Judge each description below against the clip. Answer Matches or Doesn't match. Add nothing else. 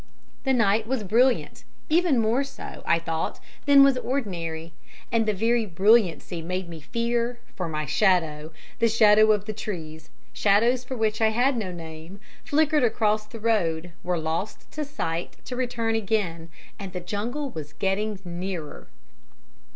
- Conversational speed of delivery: Matches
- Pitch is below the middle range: Doesn't match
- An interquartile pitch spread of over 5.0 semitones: Matches